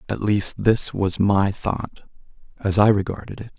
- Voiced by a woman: No, male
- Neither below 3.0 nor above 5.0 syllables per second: Yes, 4.1 syllables/s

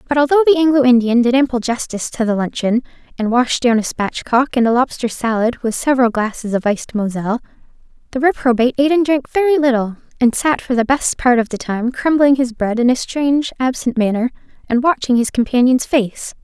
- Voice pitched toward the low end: No, very high, 250 Hz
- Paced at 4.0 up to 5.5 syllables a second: No, 5.9 syllables/s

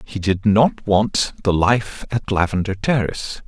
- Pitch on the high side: No, low, 100 Hz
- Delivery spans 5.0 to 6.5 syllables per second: No, 4.1 syllables/s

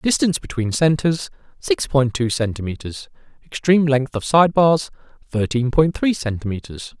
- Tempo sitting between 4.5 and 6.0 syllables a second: Yes, 4.9 syllables/s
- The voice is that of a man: Yes, male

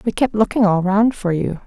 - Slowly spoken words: No, fast, 255 wpm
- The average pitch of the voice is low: No, high, 205 Hz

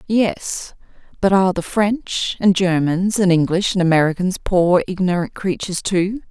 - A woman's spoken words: Yes, female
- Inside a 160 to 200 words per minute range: No, average, 145 wpm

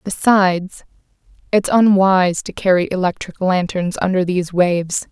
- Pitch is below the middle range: No, medium, 185 Hz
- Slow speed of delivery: Yes, slow, 115 wpm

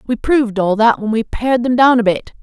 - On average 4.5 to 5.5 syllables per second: No, 5.8 syllables/s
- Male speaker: No, female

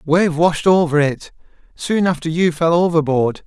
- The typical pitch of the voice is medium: Yes, medium, 165 Hz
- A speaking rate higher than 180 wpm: No, average, 140 wpm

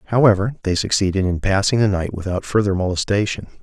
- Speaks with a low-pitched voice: Yes, low, 100 Hz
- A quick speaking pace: No, average, 165 wpm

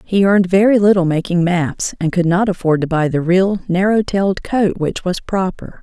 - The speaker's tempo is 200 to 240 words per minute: Yes, fast, 205 wpm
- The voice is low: No, medium, 185 Hz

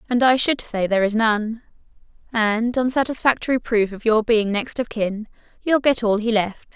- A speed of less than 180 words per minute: No, average, 195 wpm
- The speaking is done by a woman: Yes, female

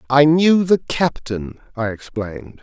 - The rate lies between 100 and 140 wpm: Yes, slow, 135 wpm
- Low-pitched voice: Yes, low, 130 Hz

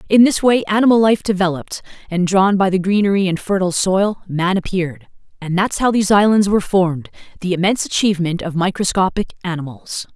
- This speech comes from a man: No, female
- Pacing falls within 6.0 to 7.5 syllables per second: Yes, 6.1 syllables/s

